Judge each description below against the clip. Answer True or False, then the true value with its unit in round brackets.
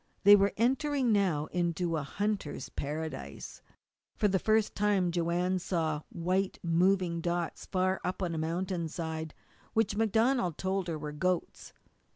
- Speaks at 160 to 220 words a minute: False (145 wpm)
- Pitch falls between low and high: True (180 Hz)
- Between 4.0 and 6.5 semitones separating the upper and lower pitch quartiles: False (3.3 semitones)